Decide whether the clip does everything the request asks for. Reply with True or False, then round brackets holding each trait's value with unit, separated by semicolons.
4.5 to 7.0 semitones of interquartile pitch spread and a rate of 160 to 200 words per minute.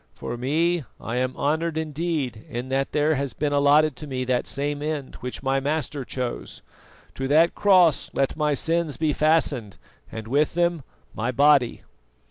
False (3.4 semitones; 165 wpm)